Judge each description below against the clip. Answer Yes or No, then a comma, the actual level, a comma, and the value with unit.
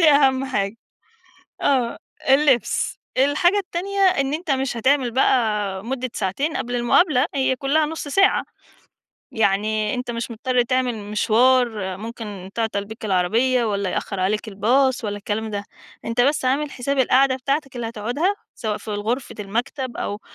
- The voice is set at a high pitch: Yes, high, 245 Hz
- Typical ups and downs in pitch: Yes, average, 4.2 semitones